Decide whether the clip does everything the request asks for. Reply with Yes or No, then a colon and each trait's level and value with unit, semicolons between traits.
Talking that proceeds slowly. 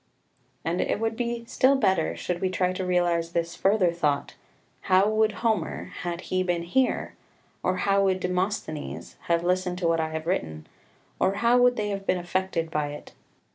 No: average, 185 wpm